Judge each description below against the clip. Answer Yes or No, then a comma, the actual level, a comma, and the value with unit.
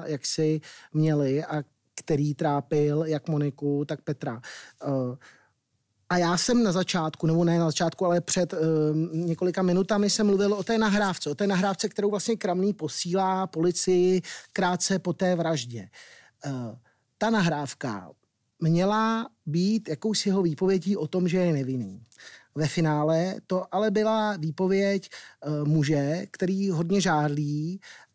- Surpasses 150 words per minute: No, average, 140 wpm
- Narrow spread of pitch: No, average, 4.3 semitones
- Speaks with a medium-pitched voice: Yes, medium, 170 Hz